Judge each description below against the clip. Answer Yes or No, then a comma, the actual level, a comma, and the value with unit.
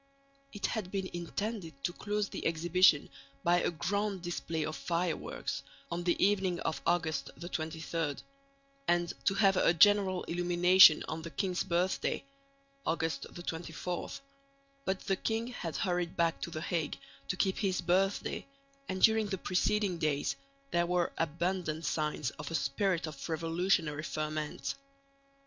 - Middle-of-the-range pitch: Yes, medium, 175 Hz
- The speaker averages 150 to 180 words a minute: No, average, 140 wpm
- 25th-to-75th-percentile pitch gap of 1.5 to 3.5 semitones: Yes, average, 2.7 semitones